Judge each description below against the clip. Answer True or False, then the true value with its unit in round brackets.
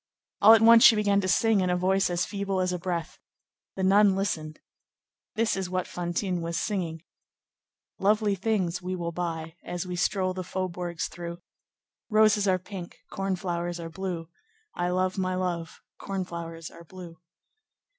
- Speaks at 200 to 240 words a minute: False (165 wpm)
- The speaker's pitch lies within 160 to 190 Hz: True (185 Hz)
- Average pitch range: False (2.2 semitones)